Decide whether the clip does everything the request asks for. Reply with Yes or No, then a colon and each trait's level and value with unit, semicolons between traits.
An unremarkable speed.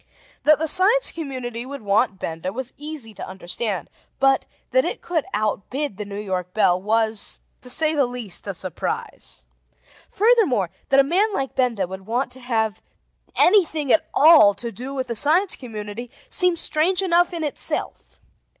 Yes: average, 165 wpm